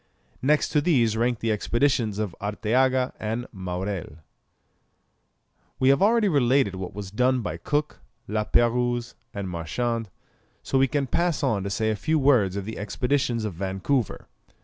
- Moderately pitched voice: No, low, 120 Hz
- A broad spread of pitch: No, average, 4.6 semitones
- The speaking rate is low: No, average, 155 wpm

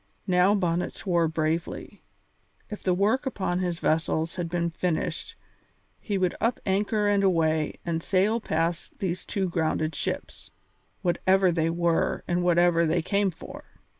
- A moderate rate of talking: Yes, average, 145 wpm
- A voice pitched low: No, medium, 175 Hz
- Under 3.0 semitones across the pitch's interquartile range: Yes, narrow, 2.6 semitones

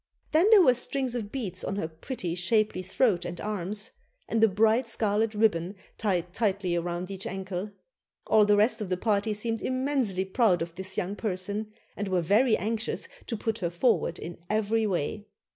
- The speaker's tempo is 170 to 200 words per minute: Yes, average, 180 wpm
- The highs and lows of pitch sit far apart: No, average, 3.4 semitones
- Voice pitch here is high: Yes, high, 205 Hz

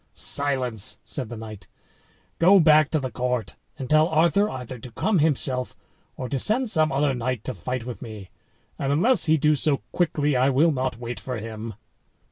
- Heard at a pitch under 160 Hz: Yes, low, 135 Hz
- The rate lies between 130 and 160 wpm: No, average, 180 wpm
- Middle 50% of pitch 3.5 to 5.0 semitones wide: Yes, average, 4.2 semitones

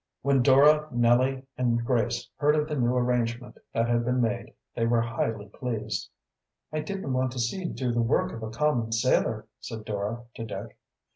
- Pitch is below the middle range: Yes, low, 120 Hz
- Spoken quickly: No, average, 190 wpm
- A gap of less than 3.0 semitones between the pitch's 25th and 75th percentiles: Yes, narrow, 2.4 semitones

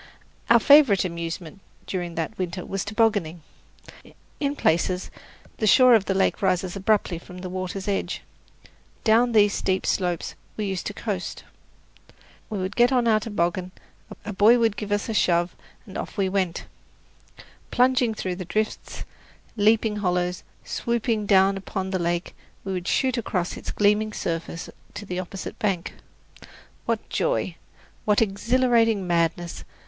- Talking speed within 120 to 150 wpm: Yes, average, 145 wpm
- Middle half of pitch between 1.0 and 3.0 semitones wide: No, average, 3.4 semitones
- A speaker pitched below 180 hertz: No, high, 195 Hz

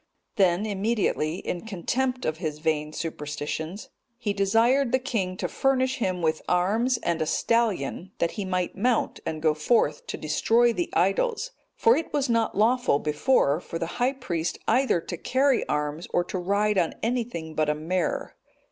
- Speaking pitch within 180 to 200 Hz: Yes, high, 190 Hz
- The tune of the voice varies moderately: No, wide, 6.9 semitones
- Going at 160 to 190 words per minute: Yes, average, 170 wpm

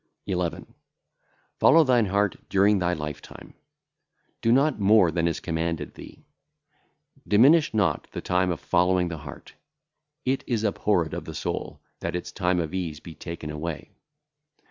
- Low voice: Yes, very low, 90 Hz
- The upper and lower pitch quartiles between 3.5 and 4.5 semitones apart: Yes, average, 4.0 semitones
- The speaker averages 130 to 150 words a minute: Yes, average, 145 wpm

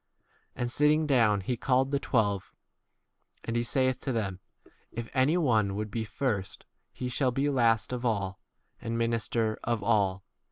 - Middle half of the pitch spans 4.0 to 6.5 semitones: No, average, 3.5 semitones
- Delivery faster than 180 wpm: No, average, 160 wpm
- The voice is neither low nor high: No, low, 115 Hz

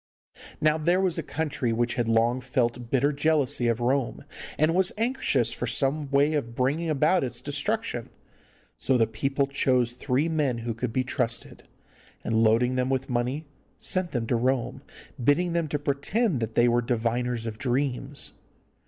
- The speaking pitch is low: Yes, low, 130 Hz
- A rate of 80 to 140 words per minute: No, average, 170 wpm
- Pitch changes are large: No, average, 3.9 semitones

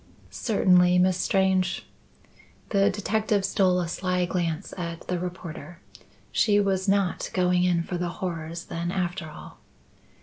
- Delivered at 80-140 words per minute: Yes, slow, 135 wpm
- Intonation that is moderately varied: No, narrow, 1.7 semitones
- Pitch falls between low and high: Yes, medium, 180 Hz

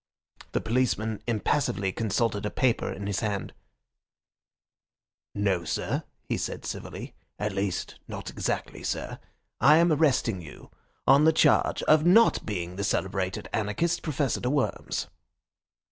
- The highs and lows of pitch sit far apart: Yes, wide, 6.2 semitones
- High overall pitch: No, low, 110 Hz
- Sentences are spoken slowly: Yes, slow, 130 wpm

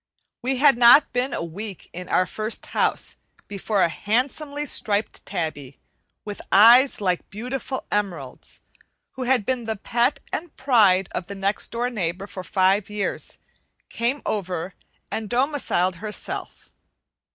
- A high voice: Yes, high, 210 Hz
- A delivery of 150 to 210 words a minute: No, average, 140 wpm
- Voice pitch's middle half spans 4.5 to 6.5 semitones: Yes, average, 4.8 semitones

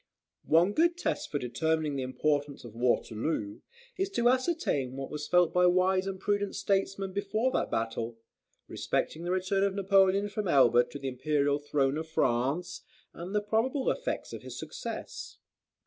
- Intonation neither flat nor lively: No, wide, 6.4 semitones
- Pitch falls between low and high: Yes, medium, 175 Hz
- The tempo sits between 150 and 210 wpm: Yes, average, 165 wpm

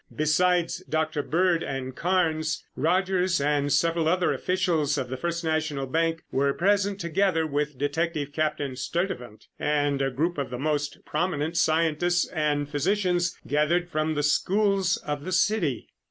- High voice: No, medium, 160 Hz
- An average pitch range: Yes, average, 3.4 semitones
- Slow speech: No, average, 145 wpm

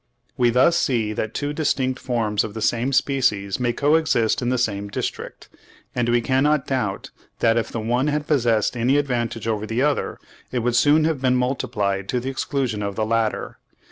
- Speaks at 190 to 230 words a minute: Yes, average, 195 wpm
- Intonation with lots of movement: No, average, 3.4 semitones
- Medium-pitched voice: No, low, 120 Hz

